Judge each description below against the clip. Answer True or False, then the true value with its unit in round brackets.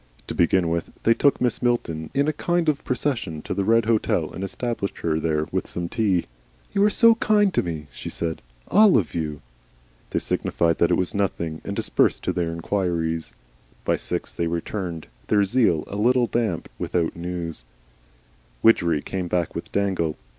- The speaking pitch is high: False (90 Hz)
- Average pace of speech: True (180 wpm)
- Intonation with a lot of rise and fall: True (6.0 semitones)